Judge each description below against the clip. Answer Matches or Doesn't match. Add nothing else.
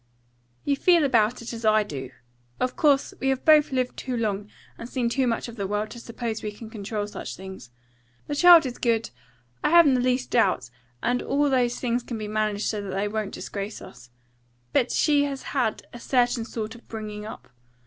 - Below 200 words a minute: Doesn't match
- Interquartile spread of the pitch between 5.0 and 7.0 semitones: Doesn't match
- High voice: Matches